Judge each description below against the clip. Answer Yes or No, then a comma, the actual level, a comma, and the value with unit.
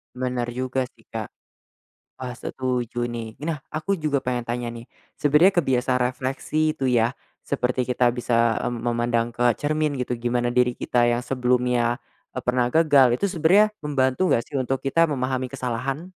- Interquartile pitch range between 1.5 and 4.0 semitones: Yes, narrow, 2.4 semitones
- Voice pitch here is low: Yes, low, 125 Hz